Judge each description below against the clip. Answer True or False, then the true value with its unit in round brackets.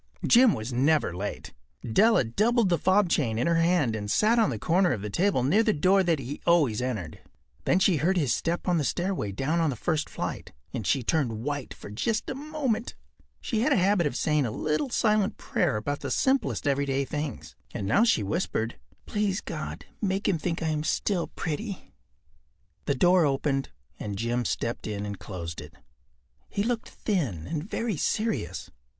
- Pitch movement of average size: False (8.3 semitones)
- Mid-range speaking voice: True (155 Hz)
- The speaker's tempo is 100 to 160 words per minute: False (190 wpm)